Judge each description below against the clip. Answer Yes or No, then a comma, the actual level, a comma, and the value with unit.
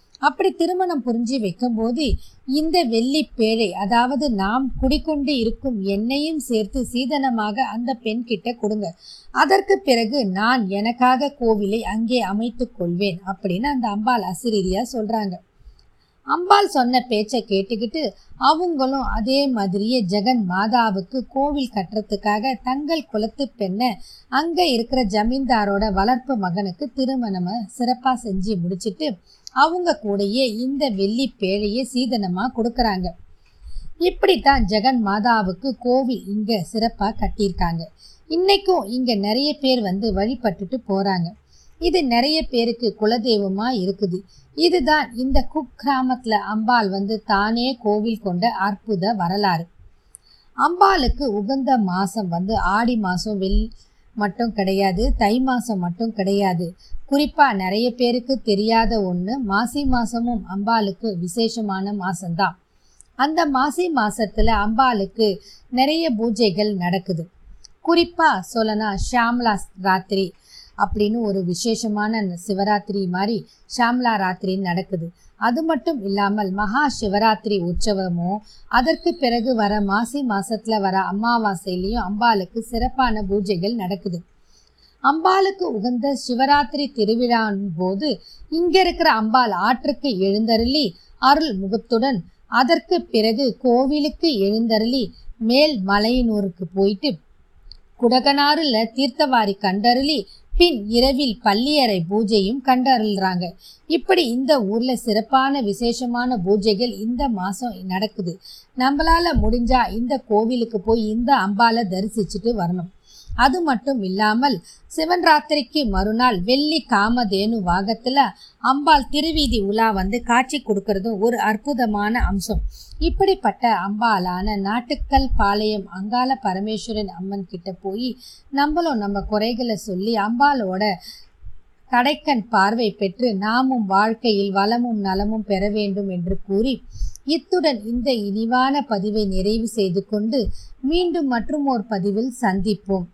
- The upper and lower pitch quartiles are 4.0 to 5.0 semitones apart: Yes, average, 4.5 semitones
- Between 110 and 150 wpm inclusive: No, average, 100 wpm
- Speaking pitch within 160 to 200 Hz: No, high, 225 Hz